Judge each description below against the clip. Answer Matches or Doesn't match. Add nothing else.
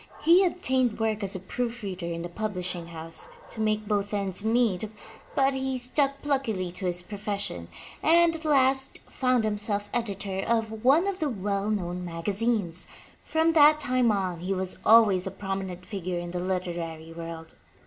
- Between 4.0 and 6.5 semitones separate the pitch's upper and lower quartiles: Matches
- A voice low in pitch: Doesn't match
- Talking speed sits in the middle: Matches